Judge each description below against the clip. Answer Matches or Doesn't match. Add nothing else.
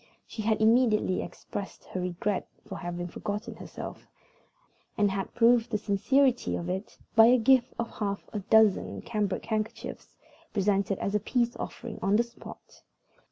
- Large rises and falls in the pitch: Doesn't match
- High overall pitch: Matches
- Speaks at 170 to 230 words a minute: Doesn't match